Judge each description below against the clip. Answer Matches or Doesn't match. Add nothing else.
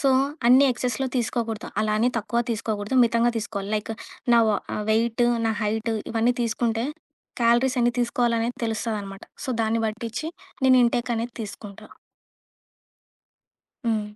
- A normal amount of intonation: Doesn't match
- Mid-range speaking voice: Doesn't match